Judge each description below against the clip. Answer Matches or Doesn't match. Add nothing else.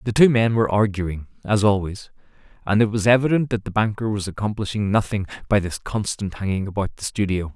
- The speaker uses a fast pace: Doesn't match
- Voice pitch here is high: Doesn't match